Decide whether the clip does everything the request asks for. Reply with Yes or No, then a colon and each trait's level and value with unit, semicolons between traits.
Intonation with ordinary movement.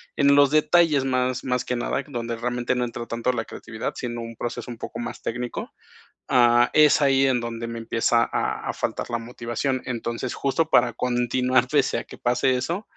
No: narrow, 2.0 semitones